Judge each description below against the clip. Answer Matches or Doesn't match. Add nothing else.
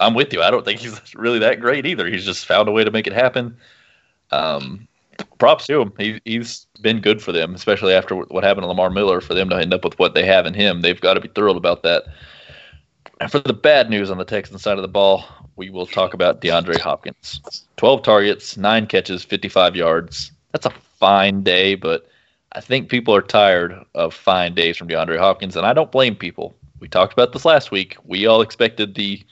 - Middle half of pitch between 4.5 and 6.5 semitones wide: Doesn't match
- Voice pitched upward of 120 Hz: Doesn't match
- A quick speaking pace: Matches